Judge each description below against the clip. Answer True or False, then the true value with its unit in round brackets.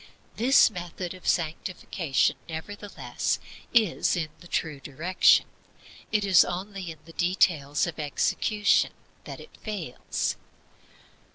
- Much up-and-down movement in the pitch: False (3.7 semitones)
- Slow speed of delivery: True (110 wpm)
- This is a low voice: False (175 Hz)